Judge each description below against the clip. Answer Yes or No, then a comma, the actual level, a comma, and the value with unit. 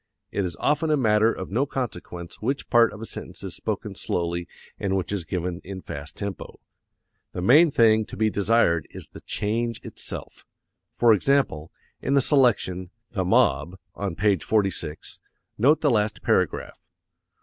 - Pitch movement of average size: Yes, average, 4.6 semitones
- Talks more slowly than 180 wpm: Yes, average, 160 wpm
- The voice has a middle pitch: No, low, 105 Hz